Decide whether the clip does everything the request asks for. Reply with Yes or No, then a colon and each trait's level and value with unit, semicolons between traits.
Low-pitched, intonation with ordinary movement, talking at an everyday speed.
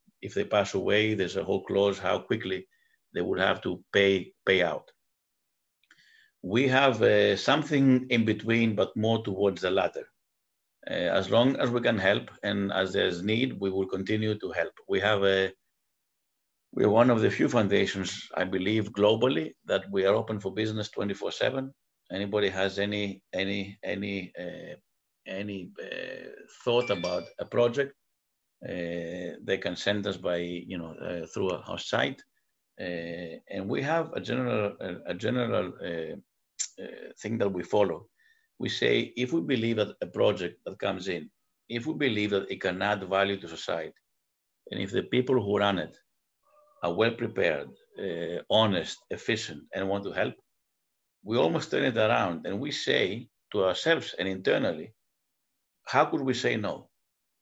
Yes: low, 105 Hz; average, 4.2 semitones; average, 165 wpm